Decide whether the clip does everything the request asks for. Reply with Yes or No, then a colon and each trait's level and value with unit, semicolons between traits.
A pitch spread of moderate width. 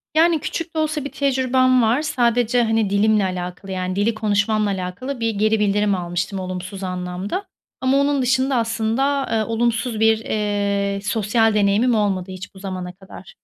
Yes: average, 4.2 semitones